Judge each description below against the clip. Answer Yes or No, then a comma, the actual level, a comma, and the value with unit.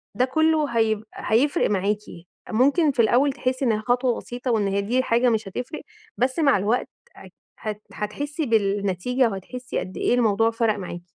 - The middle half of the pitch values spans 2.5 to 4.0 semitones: Yes, average, 3.6 semitones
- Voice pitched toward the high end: Yes, high, 235 Hz